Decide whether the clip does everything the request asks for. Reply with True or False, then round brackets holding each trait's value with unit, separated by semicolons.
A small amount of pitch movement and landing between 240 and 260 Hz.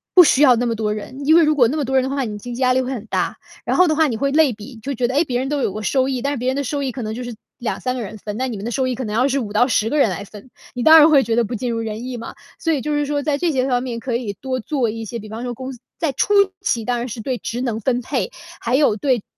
False (3.4 semitones; 255 Hz)